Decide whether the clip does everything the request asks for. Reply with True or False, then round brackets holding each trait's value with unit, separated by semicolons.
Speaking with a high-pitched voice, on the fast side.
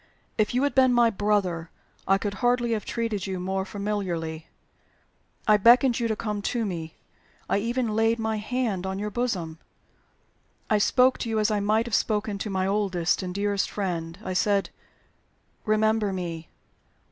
False (210 Hz; 170 wpm)